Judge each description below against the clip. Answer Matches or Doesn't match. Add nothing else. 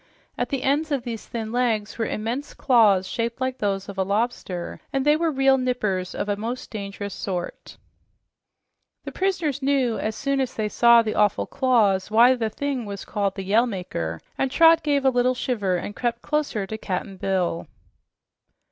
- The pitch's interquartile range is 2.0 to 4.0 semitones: Doesn't match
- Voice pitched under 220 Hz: Doesn't match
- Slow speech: Doesn't match